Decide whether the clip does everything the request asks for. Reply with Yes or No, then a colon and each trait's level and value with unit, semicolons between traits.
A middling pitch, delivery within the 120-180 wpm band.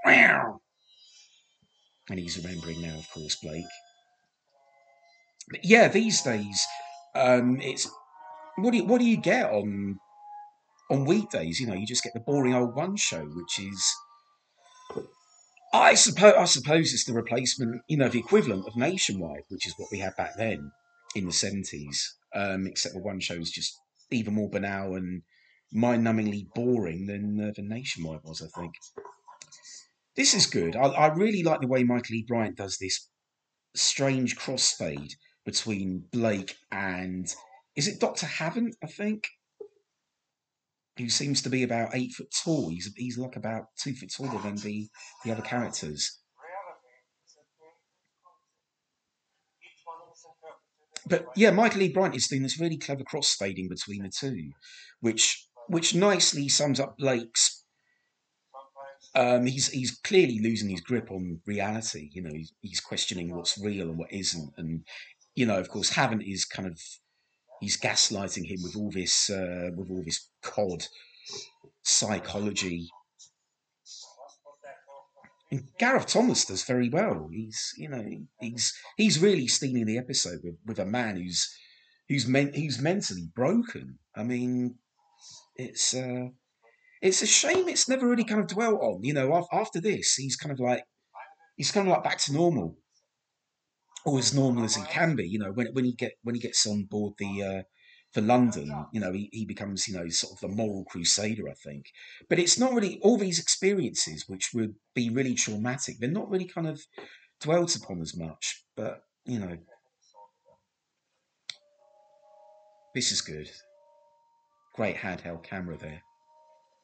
No: low, 125 Hz; average, 155 wpm